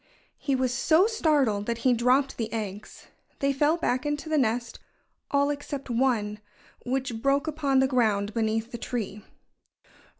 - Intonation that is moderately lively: Yes, average, 4.0 semitones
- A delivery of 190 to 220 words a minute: No, average, 155 wpm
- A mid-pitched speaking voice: No, very high, 255 Hz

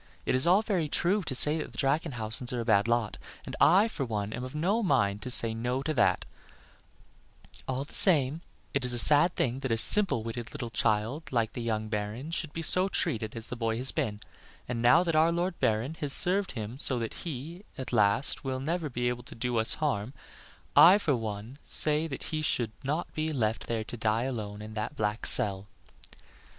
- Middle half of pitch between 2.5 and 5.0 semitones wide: No, wide, 5.6 semitones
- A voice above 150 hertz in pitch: No, low, 125 Hz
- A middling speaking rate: No, fast, 210 wpm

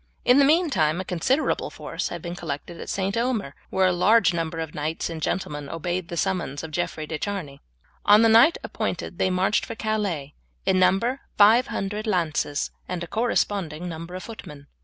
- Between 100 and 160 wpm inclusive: No, average, 185 wpm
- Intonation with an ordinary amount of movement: Yes, average, 4.8 semitones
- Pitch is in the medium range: Yes, medium, 180 Hz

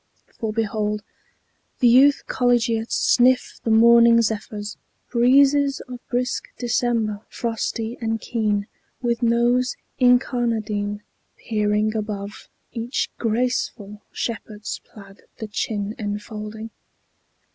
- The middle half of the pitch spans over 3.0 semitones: No, narrow, 2.4 semitones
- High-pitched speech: Yes, high, 225 Hz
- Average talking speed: No, slow, 95 wpm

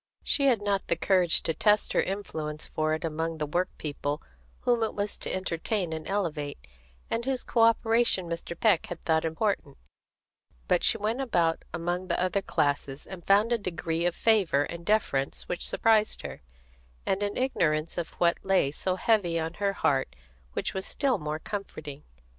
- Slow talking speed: No, average, 175 wpm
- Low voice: No, medium, 175 Hz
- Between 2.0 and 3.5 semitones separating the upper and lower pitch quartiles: No, average, 4.5 semitones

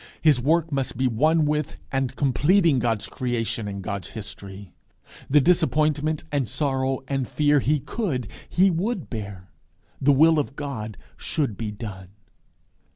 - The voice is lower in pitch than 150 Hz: Yes, low, 135 Hz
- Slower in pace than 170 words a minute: Yes, average, 145 wpm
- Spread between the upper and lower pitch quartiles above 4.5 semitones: Yes, average, 5.1 semitones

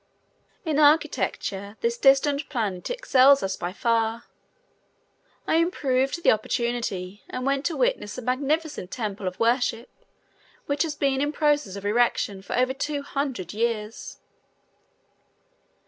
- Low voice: No, very high, 255 Hz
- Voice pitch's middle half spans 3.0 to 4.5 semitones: No, average, 5.2 semitones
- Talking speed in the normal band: No, slow, 130 wpm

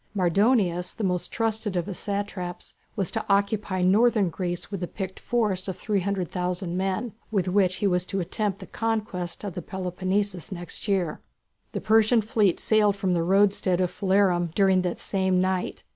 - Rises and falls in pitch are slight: Yes, narrow, 2.3 semitones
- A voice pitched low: No, high, 190 Hz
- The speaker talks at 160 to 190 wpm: Yes, average, 170 wpm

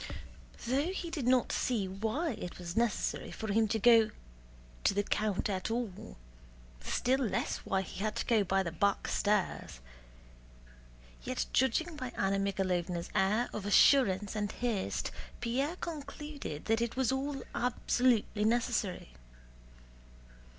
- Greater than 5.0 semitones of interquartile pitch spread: No, average, 4.6 semitones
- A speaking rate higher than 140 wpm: No, slow, 135 wpm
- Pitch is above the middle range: Yes, high, 220 Hz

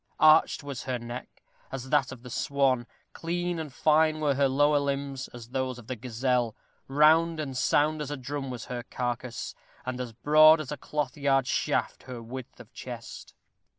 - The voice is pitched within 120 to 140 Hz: Yes, low, 135 Hz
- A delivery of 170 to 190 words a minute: Yes, average, 185 wpm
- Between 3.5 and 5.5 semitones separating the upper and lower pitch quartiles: No, average, 3.0 semitones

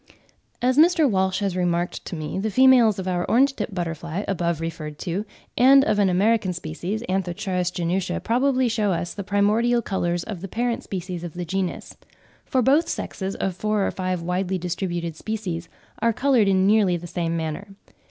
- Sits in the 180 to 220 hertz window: Yes, high, 190 Hz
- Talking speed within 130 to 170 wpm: No, average, 180 wpm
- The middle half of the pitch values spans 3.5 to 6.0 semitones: Yes, average, 3.9 semitones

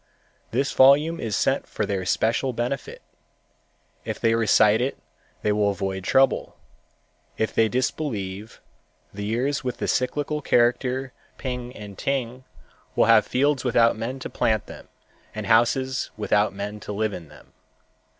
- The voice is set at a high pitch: No, low, 115 Hz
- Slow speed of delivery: No, average, 145 wpm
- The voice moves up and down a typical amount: Yes, average, 3.9 semitones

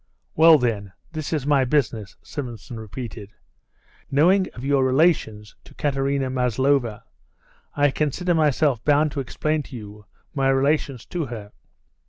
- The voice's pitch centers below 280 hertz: Yes, low, 135 Hz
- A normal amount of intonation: Yes, average, 4.1 semitones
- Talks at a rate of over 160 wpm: No, slow, 135 wpm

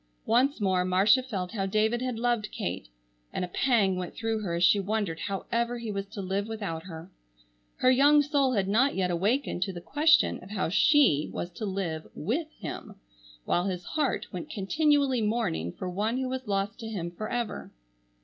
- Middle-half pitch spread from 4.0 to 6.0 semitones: Yes, average, 4.9 semitones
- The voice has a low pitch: No, high, 210 Hz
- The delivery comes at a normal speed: Yes, average, 190 wpm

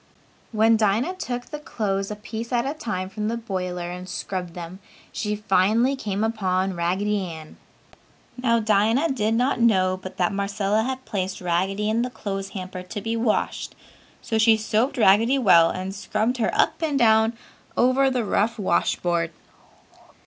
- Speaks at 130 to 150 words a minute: No, average, 165 wpm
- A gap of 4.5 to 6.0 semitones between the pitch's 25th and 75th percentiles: No, average, 3.7 semitones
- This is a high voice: Yes, high, 210 Hz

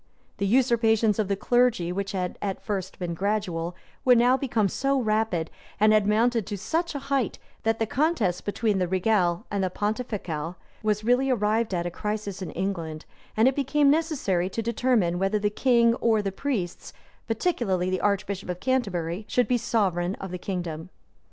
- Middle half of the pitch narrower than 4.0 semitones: No, average, 4.4 semitones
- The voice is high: Yes, high, 210 Hz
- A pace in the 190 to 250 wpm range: No, average, 175 wpm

